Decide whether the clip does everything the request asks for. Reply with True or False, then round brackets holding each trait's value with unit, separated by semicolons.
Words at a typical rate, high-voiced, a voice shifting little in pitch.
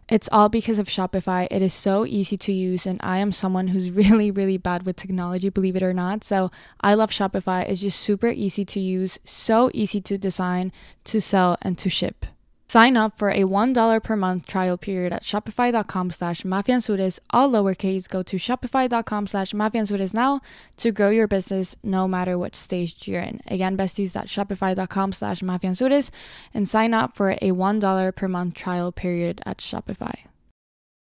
True (175 wpm; 195 Hz; 2.3 semitones)